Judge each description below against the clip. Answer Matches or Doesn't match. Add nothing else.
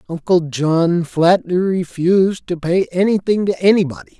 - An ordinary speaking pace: Doesn't match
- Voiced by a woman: Doesn't match